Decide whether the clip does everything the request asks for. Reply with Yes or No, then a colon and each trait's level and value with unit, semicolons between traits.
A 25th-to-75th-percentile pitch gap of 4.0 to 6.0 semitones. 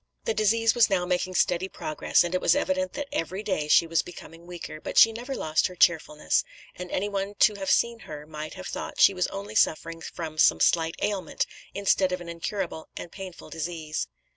No: average, 3.6 semitones